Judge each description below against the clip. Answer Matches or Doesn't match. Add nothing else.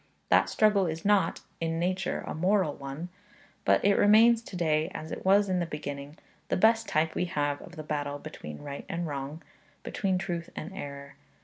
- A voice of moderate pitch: Matches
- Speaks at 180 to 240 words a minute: Matches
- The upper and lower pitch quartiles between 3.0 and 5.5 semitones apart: Matches